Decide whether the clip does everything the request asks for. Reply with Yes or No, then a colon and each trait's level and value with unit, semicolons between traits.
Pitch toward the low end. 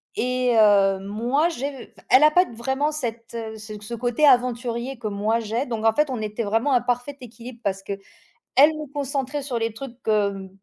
No: high, 240 Hz